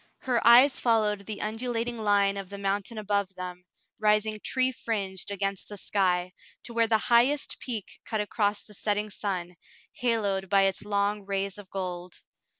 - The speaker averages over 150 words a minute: Yes, average, 160 wpm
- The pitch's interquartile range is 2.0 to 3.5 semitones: Yes, narrow, 2.4 semitones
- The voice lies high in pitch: Yes, high, 205 Hz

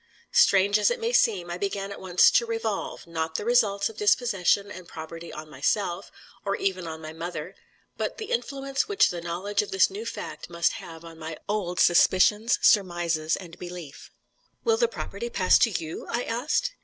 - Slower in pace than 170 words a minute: No, average, 185 wpm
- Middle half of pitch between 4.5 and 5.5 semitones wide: Yes, average, 5.2 semitones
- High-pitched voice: Yes, high, 195 Hz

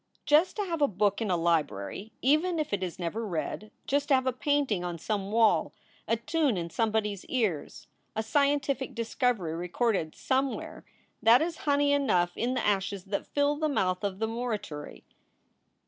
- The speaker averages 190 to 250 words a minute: No, average, 180 wpm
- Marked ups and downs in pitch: Yes, wide, 6.8 semitones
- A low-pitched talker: No, high, 225 Hz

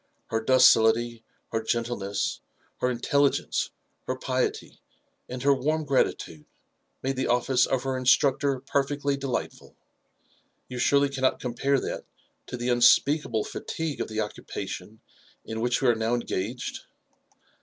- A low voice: Yes, low, 125 Hz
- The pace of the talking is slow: Yes, slow, 130 wpm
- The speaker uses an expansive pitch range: No, average, 2.8 semitones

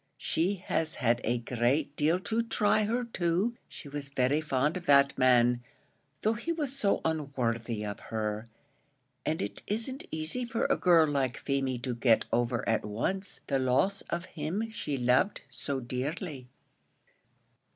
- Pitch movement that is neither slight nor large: No, wide, 7.2 semitones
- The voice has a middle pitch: Yes, medium, 145 Hz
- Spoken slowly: No, average, 155 wpm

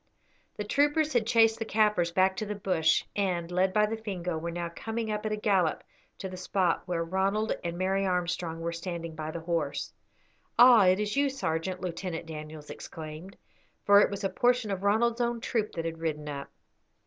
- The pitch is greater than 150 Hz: Yes, high, 190 Hz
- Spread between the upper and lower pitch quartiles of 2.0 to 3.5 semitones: No, average, 4.2 semitones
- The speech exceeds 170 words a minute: Yes, average, 195 wpm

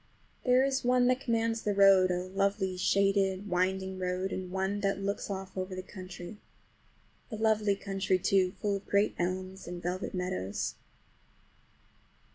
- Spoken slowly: No, average, 155 wpm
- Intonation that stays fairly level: Yes, narrow, 1.7 semitones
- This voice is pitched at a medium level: No, high, 195 Hz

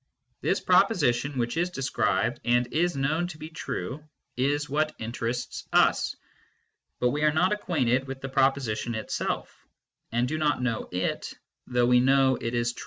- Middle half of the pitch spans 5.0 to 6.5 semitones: No, average, 3.9 semitones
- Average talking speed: Yes, average, 170 wpm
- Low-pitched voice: Yes, low, 130 Hz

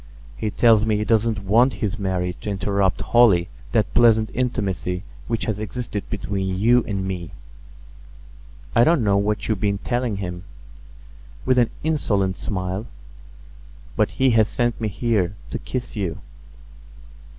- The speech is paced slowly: No, average, 145 wpm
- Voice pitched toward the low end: Yes, low, 105 Hz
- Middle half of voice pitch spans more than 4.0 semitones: No, average, 3.5 semitones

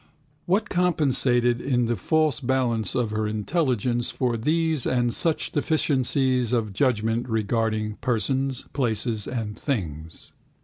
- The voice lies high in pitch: No, low, 120 Hz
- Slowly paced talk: Yes, slow, 120 wpm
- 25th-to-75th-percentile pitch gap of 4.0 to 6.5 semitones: No, average, 3.6 semitones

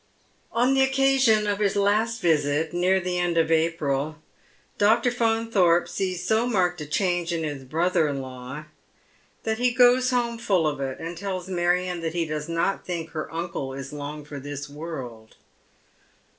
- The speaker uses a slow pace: No, average, 170 wpm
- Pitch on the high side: No, medium, 175 Hz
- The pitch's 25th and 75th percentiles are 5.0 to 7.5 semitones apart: Yes, wide, 5.6 semitones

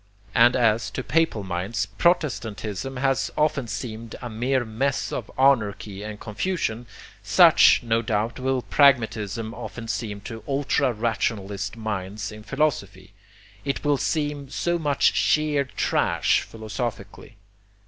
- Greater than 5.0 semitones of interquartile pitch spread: No, average, 4.2 semitones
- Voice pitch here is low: Yes, low, 115 Hz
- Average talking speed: No, slow, 125 wpm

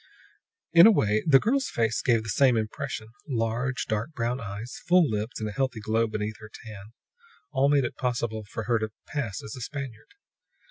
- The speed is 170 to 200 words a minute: Yes, average, 190 wpm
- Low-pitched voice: Yes, low, 115 Hz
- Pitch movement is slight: No, average, 3.7 semitones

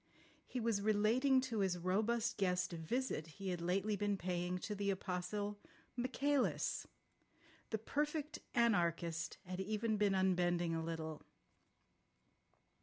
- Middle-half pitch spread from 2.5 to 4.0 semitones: No, average, 4.4 semitones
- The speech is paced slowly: Yes, slow, 125 wpm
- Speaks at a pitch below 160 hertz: No, high, 200 Hz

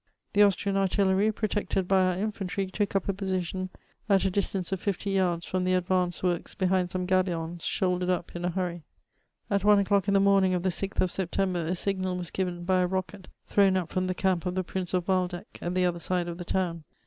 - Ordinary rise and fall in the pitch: No, narrow, 1.5 semitones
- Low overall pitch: No, medium, 185 Hz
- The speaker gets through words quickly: Yes, fast, 225 wpm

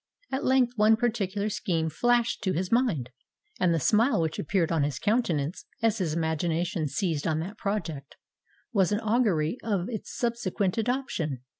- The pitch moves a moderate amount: No, wide, 6.0 semitones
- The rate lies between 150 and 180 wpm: Yes, average, 160 wpm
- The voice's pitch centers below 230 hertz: Yes, high, 190 Hz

